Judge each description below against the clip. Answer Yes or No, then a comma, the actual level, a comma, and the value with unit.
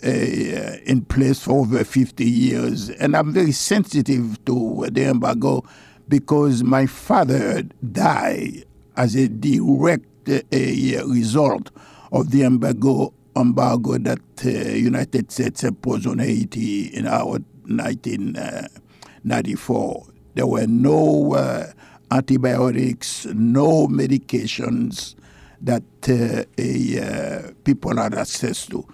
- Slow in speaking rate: Yes, slow, 110 wpm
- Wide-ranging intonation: No, narrow, 2.4 semitones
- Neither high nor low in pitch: No, low, 130 Hz